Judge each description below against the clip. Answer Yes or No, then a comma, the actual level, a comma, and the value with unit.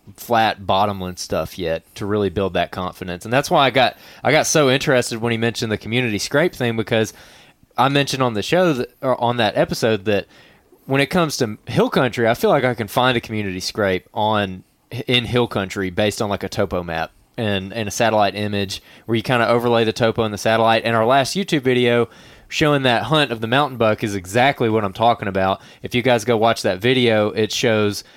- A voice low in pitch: Yes, low, 115 Hz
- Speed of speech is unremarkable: No, fast, 220 wpm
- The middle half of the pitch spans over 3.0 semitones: Yes, average, 3.5 semitones